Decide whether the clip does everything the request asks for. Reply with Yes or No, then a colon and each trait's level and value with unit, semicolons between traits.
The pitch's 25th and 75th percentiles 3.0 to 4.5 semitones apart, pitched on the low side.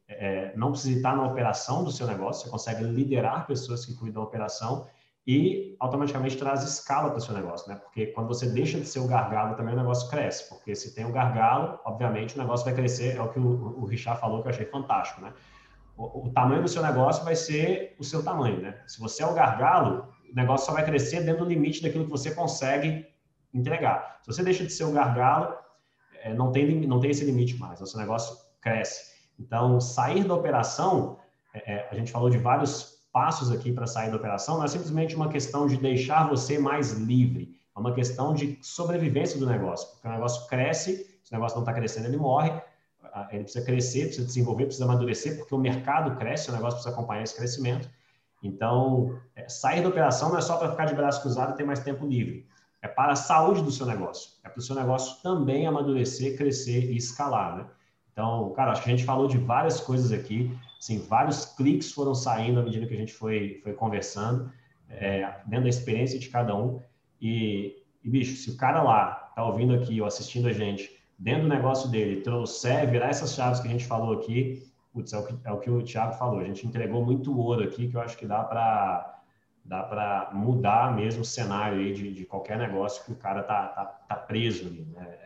Yes: average, 3.5 semitones; low, 125 Hz